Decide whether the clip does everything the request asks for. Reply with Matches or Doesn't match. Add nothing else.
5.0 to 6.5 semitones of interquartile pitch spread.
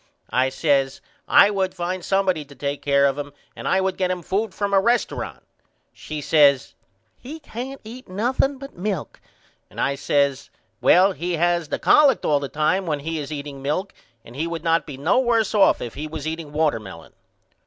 Matches